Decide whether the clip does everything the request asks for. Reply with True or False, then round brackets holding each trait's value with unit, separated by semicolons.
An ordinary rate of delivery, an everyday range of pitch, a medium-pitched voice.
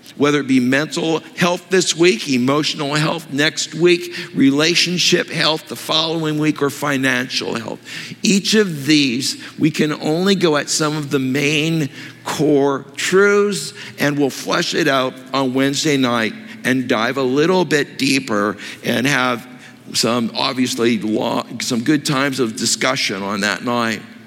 True (150 wpm; 3.7 semitones; 145 Hz)